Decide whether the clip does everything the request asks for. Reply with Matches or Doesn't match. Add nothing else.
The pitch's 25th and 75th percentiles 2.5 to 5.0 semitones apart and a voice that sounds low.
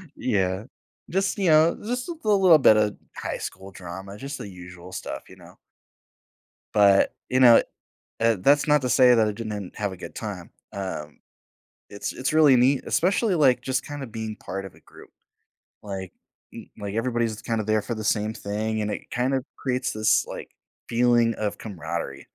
Matches